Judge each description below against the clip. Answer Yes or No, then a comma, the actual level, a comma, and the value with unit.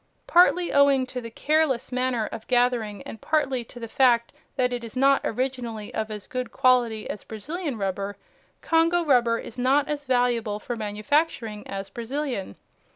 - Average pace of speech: Yes, average, 160 wpm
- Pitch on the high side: Yes, high, 245 Hz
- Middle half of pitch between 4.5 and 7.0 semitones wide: No, average, 3.6 semitones